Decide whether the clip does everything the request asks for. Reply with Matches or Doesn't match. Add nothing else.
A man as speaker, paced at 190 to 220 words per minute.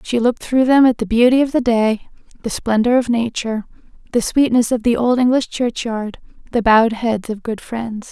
Doesn't match